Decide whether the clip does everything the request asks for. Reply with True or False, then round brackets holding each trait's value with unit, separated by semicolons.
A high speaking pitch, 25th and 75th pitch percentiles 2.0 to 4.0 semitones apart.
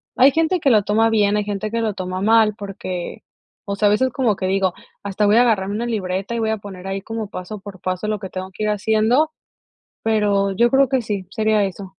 True (210 Hz; 2.5 semitones)